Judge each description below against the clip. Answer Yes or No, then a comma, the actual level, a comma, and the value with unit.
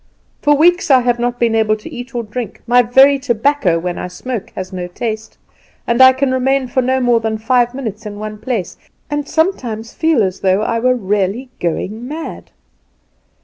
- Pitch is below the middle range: No, high, 240 Hz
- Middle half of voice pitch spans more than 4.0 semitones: No, average, 3.4 semitones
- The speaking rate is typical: Yes, average, 190 wpm